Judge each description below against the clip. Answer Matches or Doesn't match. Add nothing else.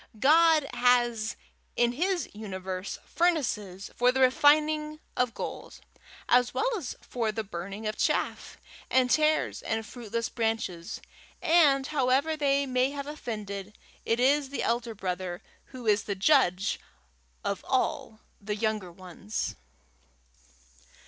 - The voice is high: Matches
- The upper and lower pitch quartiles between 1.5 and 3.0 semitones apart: Doesn't match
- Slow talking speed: Matches